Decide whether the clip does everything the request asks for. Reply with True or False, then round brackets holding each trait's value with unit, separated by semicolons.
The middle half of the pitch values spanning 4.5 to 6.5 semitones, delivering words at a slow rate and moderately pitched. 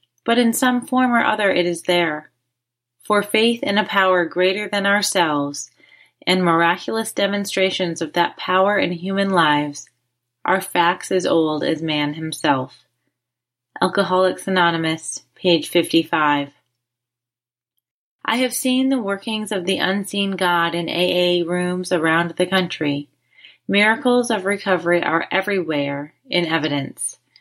True (5.0 semitones; 130 wpm; 175 Hz)